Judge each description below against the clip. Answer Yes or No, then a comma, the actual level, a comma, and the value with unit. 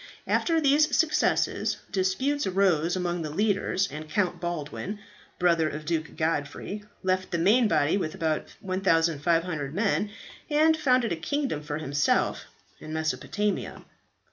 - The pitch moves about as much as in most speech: Yes, average, 4.6 semitones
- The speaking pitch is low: No, medium, 180 Hz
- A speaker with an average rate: No, slow, 130 wpm